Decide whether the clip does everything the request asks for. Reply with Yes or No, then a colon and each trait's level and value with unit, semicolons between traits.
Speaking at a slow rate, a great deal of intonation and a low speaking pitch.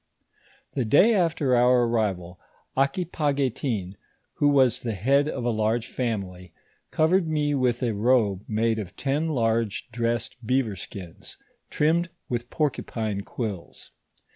No: slow, 125 wpm; average, 4.6 semitones; low, 120 Hz